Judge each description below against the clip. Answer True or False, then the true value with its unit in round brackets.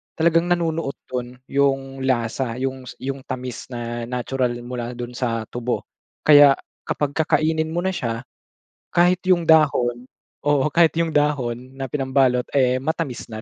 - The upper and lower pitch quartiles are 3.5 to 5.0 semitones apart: True (3.9 semitones)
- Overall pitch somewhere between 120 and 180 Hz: True (135 Hz)